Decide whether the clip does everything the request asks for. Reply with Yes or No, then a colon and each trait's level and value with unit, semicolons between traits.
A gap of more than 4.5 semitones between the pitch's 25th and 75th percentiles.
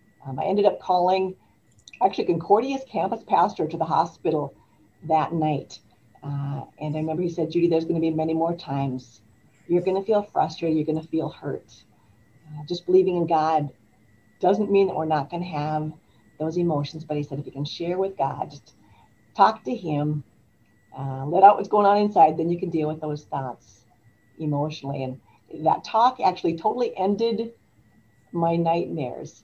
Yes: average, 5.0 semitones